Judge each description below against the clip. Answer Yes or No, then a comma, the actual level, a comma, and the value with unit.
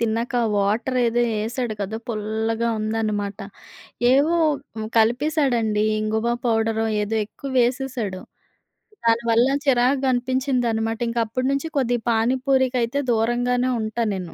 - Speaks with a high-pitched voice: Yes, high, 235 Hz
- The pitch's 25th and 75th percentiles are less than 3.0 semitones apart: Yes, narrow, 2.5 semitones